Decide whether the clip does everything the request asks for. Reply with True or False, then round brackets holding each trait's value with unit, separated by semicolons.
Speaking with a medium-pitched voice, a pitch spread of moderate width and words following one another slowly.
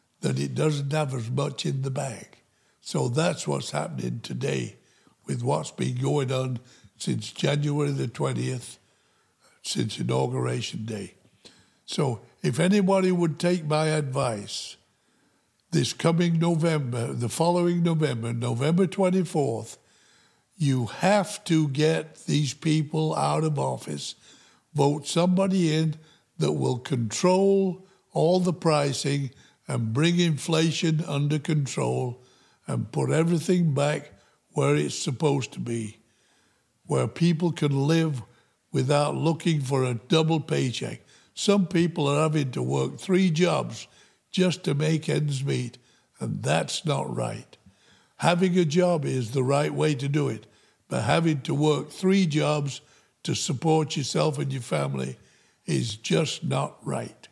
True (150 Hz; 4.8 semitones; 130 wpm)